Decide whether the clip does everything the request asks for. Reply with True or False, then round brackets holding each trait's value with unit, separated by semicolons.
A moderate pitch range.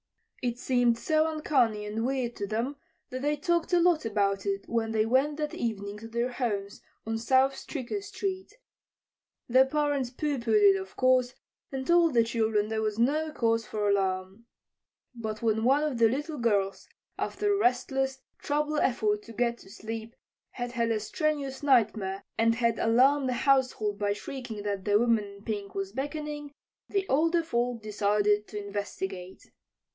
True (4.6 semitones)